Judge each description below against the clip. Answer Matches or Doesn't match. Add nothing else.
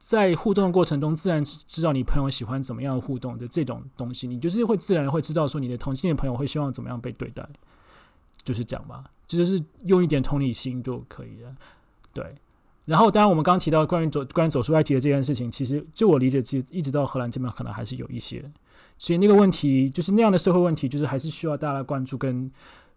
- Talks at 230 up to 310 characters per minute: Doesn't match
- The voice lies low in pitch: Doesn't match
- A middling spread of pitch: Matches